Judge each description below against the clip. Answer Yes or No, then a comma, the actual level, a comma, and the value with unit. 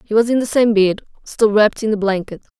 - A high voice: Yes, high, 210 Hz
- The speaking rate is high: Yes, fast, 255 wpm